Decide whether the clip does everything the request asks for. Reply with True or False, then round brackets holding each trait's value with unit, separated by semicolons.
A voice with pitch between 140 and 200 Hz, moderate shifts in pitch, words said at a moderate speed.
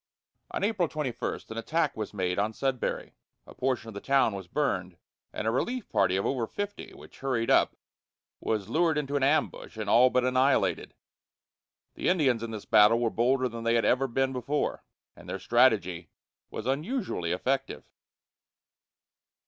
False (125 Hz; 4.1 semitones; 165 wpm)